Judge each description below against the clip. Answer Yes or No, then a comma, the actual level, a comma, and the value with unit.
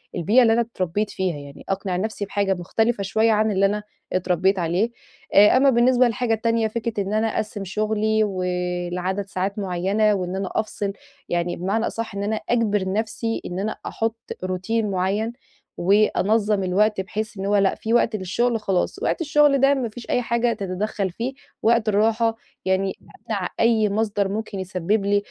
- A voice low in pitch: No, high, 210 Hz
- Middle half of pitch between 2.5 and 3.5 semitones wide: Yes, average, 2.9 semitones